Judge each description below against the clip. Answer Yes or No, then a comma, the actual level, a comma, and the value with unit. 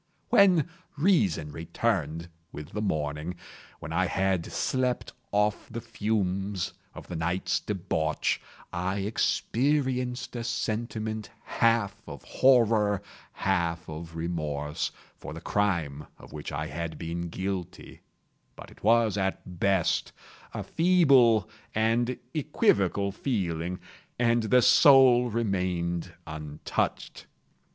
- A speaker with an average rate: No, slow, 105 wpm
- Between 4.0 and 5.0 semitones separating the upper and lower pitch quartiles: No, wide, 5.6 semitones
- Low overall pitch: Yes, low, 100 Hz